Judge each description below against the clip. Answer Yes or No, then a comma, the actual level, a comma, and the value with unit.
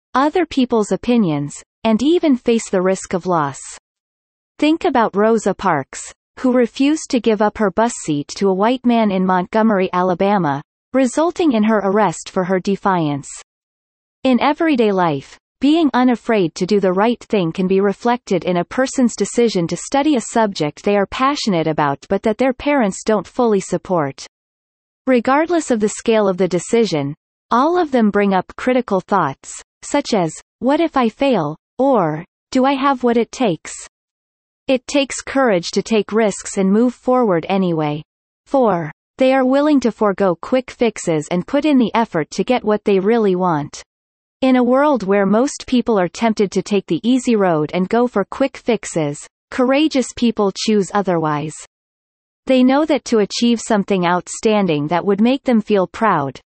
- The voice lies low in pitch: No, high, 215 Hz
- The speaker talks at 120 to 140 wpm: No, average, 170 wpm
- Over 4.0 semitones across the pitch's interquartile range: Yes, wide, 5.5 semitones